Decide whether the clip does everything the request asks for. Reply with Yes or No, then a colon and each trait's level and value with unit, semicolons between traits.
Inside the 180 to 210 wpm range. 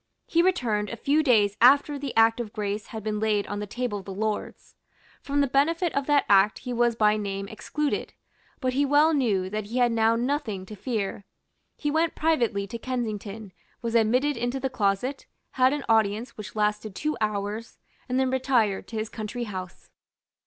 Yes: average, 190 wpm